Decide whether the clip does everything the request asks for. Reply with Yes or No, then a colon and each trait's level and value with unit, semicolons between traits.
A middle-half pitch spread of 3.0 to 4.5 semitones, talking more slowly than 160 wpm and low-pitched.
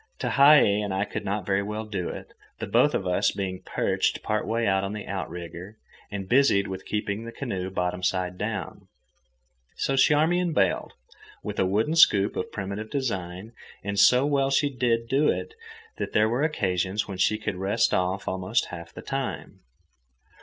No: average, 4.0 semitones; average, 175 wpm; low, 100 Hz